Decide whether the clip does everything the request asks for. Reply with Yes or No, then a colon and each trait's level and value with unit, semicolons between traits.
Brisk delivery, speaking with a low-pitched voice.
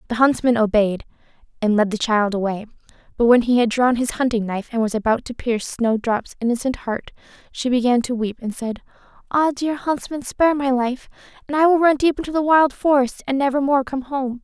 No: fast, 210 wpm; very high, 250 Hz